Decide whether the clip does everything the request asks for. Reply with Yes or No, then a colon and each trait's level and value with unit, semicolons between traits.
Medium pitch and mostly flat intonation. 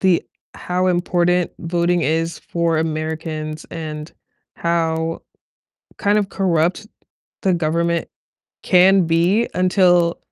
Yes: medium, 170 Hz; narrow, 1.9 semitones